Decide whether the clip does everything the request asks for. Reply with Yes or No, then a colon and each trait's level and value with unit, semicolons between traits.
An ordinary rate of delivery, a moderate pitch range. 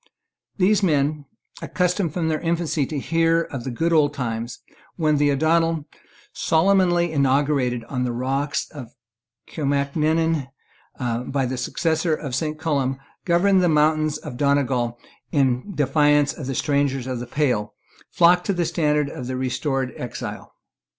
Yes: average, 145 wpm; average, 3.7 semitones